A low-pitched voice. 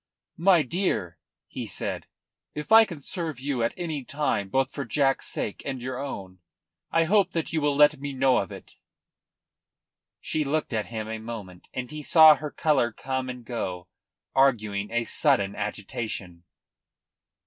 Yes: low, 130 Hz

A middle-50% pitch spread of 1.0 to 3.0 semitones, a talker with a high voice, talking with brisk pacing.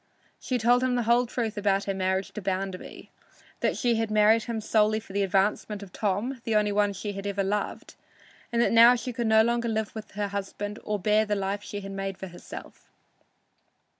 Yes: narrow, 2.4 semitones; high, 210 Hz; fast, 210 wpm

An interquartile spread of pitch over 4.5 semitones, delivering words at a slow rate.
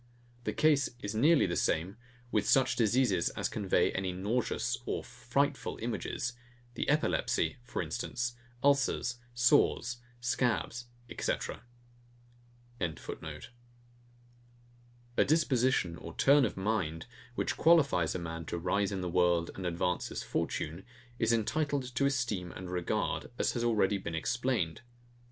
Yes: average, 5.1 semitones; slow, 130 wpm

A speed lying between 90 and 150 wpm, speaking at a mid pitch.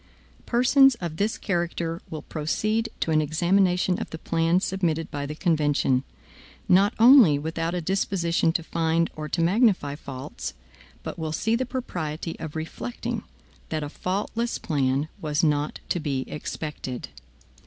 Yes: average, 145 wpm; medium, 165 Hz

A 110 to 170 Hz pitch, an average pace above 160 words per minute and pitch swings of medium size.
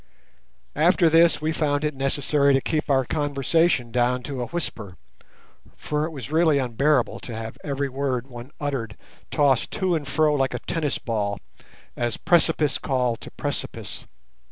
No: medium, 140 Hz; average, 155 wpm; average, 3.5 semitones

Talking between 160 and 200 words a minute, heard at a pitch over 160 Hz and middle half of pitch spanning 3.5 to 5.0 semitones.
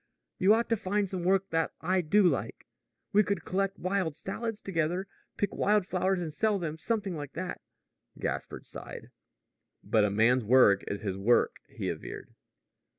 Yes: average, 165 wpm; medium, 185 Hz; average, 4.6 semitones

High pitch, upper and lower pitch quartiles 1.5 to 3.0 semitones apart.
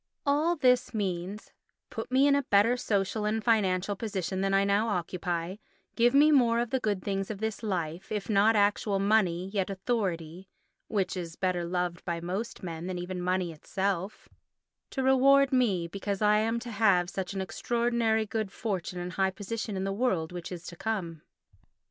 No: high, 200 Hz; average, 3.7 semitones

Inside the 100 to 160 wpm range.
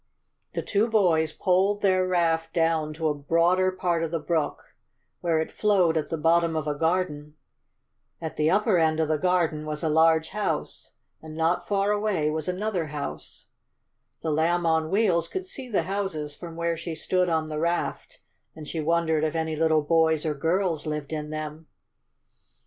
No: average, 180 wpm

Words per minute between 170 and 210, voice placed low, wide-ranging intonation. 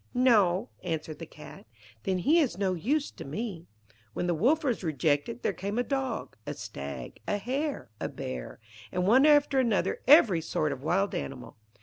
No: average, 180 wpm; high, 195 Hz; wide, 8.2 semitones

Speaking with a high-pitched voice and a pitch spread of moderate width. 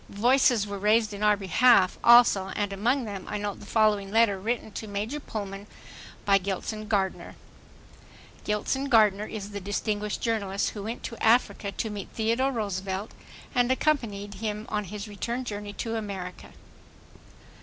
No: high, 210 Hz; narrow, 2.2 semitones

